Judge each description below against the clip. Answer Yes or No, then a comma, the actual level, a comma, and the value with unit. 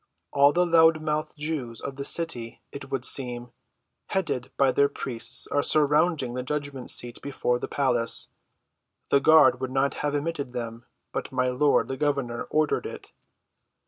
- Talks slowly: No, average, 150 wpm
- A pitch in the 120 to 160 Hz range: Yes, medium, 140 Hz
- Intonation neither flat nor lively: Yes, average, 3.1 semitones